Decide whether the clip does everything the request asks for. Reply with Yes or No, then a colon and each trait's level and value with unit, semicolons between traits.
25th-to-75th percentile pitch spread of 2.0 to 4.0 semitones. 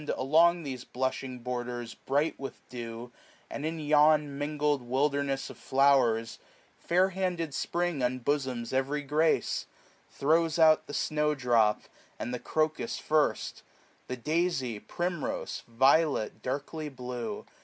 Yes: average, 3.7 semitones